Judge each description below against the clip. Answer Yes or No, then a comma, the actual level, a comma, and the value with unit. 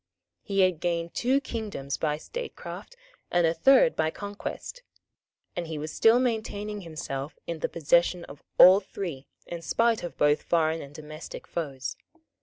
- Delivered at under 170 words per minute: Yes, average, 155 wpm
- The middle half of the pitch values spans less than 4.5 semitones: No, average, 5.1 semitones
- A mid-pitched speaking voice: Yes, medium, 170 Hz